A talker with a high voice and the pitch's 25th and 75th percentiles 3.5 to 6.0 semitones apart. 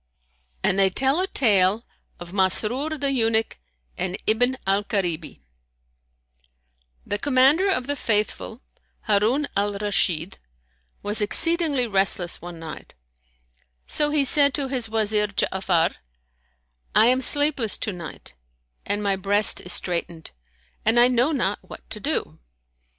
Yes: high, 215 Hz; average, 5.3 semitones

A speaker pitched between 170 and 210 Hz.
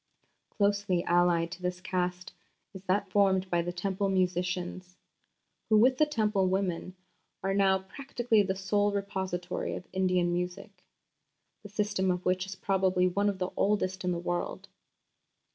Yes: high, 190 Hz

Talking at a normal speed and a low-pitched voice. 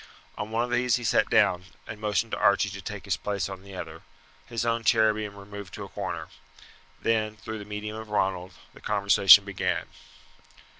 Yes: average, 195 wpm; low, 105 Hz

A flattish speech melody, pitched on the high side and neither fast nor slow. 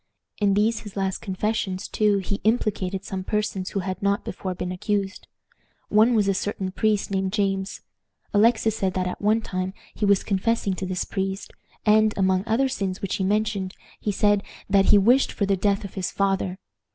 Yes: narrow, 1.9 semitones; high, 200 Hz; average, 190 wpm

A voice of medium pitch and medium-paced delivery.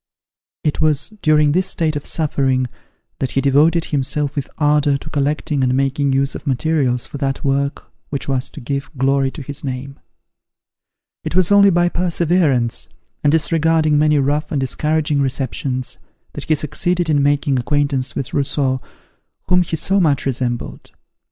Yes: medium, 145 Hz; average, 160 wpm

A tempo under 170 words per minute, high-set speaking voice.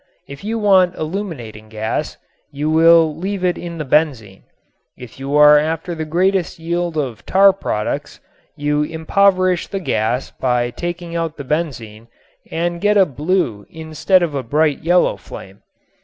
No: average, 155 wpm; medium, 160 Hz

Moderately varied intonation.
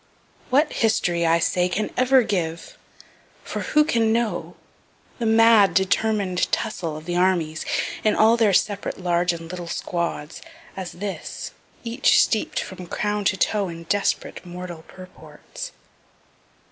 Yes: average, 4.1 semitones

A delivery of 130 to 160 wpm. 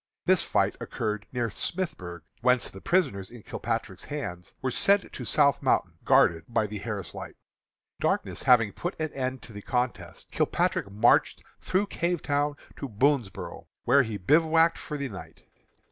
Yes: average, 155 wpm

